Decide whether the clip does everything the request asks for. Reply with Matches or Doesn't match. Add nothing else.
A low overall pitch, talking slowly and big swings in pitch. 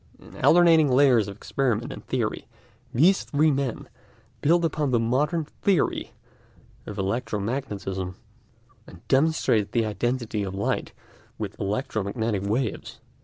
Matches